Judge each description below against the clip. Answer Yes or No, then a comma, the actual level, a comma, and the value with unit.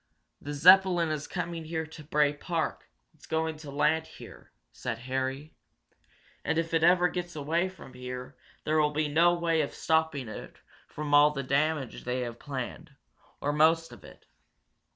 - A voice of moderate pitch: Yes, medium, 155 Hz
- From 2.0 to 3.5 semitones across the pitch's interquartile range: Yes, narrow, 2.5 semitones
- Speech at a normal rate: Yes, average, 170 wpm